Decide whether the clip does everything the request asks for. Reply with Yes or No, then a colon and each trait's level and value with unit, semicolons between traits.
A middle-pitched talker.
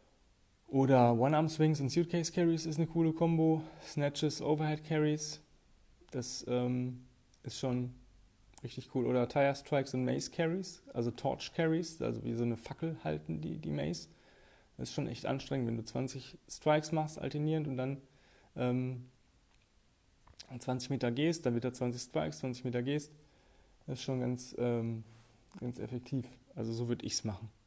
No: low, 130 Hz